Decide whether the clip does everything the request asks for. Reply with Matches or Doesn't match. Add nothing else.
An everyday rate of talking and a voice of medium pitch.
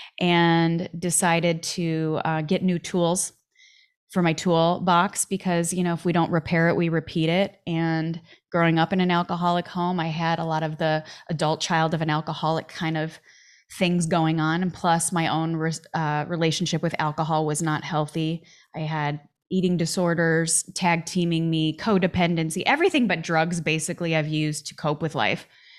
Matches